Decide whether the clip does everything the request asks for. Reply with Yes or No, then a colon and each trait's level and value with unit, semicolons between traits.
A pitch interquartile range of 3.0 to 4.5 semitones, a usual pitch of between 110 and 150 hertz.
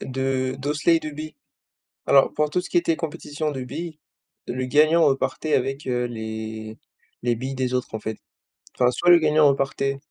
Yes: average, 3.3 semitones; low, 135 Hz